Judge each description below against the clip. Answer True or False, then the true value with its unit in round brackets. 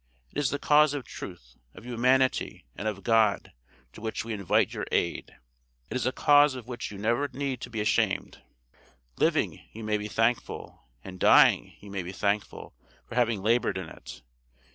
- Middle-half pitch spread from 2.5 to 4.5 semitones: True (4.0 semitones)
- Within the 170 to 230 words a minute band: True (180 wpm)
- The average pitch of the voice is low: True (115 Hz)